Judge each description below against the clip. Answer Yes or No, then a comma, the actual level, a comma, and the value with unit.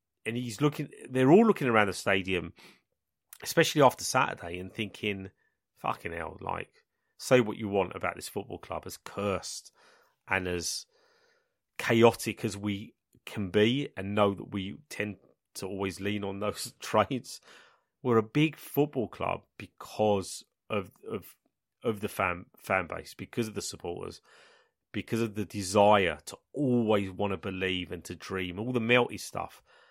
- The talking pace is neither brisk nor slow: Yes, average, 155 wpm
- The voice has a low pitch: Yes, low, 105 Hz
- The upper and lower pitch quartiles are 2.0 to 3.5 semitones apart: No, average, 4.2 semitones